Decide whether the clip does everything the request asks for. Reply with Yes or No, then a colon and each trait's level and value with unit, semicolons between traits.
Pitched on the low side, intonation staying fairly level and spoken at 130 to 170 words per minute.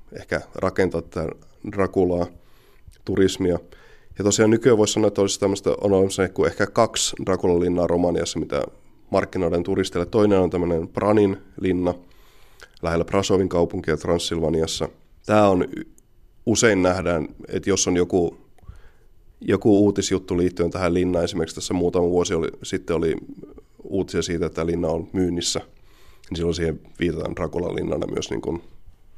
Yes: very low, 90 Hz; narrow, 2.2 semitones; average, 140 wpm